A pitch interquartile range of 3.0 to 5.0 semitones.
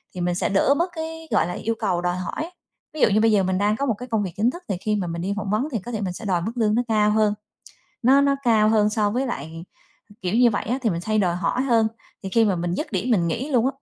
Yes: average, 4.5 semitones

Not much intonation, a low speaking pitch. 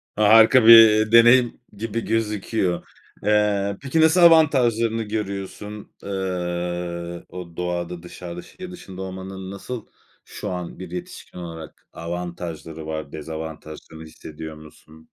No: average, 4.5 semitones; very low, 95 Hz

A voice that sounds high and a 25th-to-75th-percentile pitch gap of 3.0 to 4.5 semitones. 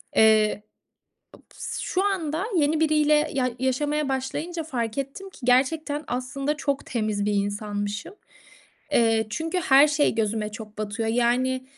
No: very high, 260 Hz; wide, 5.5 semitones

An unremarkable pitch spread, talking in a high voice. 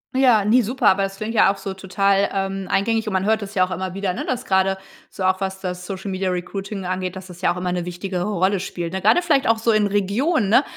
No: narrow, 2.3 semitones; high, 195 Hz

